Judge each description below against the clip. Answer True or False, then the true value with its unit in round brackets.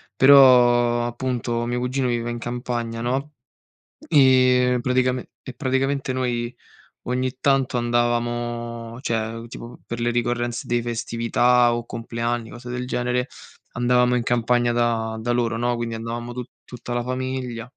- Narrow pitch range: True (1.1 semitones)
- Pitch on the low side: True (120 Hz)